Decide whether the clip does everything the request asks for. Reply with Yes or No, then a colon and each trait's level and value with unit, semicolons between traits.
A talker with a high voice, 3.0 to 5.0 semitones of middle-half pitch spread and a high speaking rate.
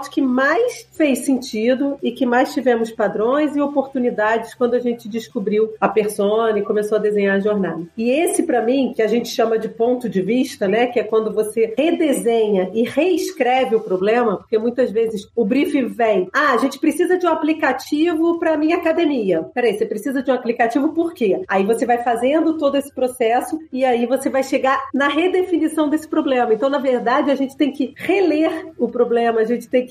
Yes: very high, 250 Hz; average, 4.1 semitones; fast, 200 wpm